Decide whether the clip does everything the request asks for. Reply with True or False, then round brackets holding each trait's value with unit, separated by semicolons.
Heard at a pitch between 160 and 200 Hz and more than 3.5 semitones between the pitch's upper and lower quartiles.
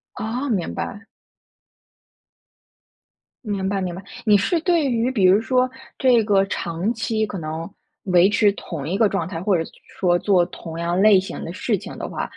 True (195 Hz; 3.9 semitones)